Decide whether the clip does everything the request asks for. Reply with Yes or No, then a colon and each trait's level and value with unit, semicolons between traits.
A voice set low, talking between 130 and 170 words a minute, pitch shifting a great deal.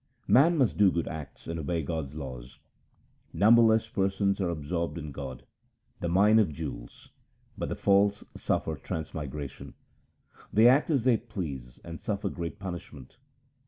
Yes: very low, 85 Hz; average, 150 wpm; wide, 5.7 semitones